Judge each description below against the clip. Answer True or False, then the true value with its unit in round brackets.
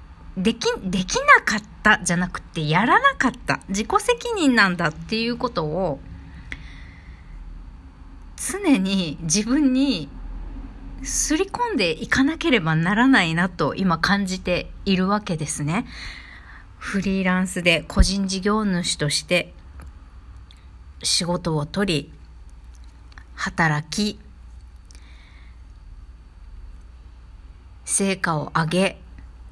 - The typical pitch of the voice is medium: True (165 Hz)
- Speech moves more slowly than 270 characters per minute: True (190 characters per minute)